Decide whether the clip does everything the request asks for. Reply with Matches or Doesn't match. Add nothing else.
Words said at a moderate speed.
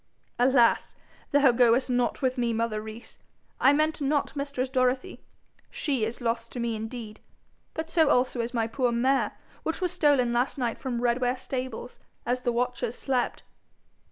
Matches